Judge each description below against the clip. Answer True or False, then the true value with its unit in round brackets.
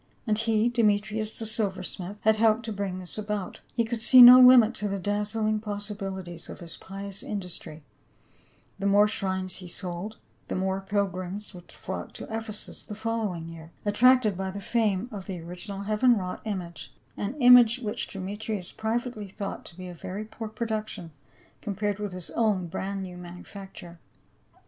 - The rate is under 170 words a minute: False (175 wpm)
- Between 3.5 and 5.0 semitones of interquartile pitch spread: False (2.8 semitones)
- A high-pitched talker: True (205 Hz)